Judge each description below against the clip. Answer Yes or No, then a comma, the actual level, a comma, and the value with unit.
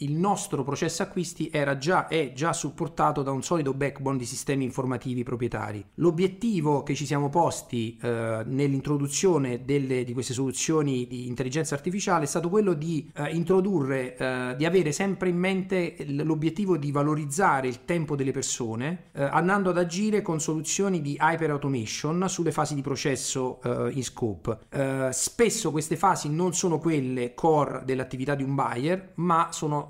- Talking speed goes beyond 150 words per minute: Yes, average, 160 wpm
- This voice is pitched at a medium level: Yes, medium, 145 Hz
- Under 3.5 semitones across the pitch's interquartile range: No, average, 4.4 semitones